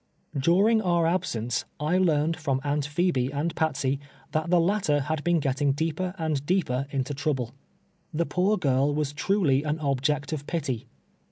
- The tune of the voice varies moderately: Yes, average, 3.7 semitones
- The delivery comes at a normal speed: Yes, average, 160 wpm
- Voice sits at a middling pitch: Yes, medium, 150 Hz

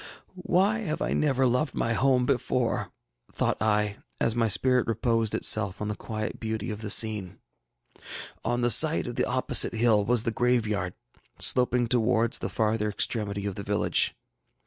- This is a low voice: Yes, low, 115 Hz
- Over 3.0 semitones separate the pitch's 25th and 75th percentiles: No, narrow, 2.6 semitones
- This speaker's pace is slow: No, average, 165 wpm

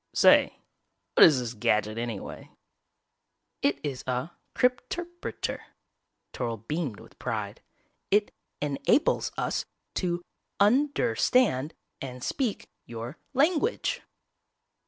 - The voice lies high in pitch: No, medium, 150 Hz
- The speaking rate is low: Yes, slow, 115 wpm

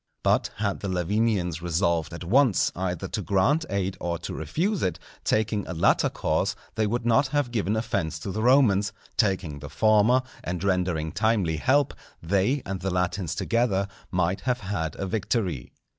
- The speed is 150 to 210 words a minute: Yes, average, 170 wpm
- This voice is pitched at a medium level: No, low, 100 Hz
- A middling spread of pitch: Yes, average, 4.3 semitones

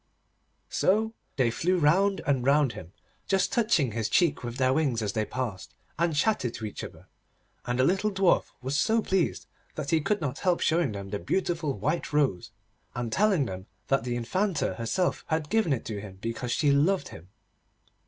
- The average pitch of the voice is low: No, medium, 145 Hz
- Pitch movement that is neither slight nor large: No, wide, 7.5 semitones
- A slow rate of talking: No, average, 185 wpm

